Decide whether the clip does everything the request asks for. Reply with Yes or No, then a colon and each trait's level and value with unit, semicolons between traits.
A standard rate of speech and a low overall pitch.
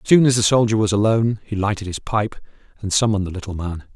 No: fast, 245 wpm; low, 105 Hz